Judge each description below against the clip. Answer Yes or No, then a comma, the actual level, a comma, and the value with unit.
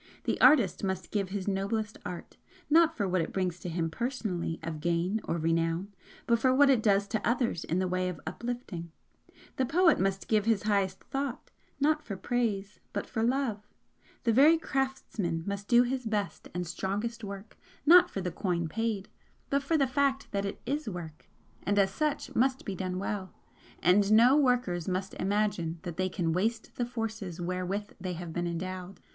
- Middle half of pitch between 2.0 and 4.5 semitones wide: No, average, 4.9 semitones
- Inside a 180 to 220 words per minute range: Yes, average, 185 wpm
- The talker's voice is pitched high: Yes, high, 200 Hz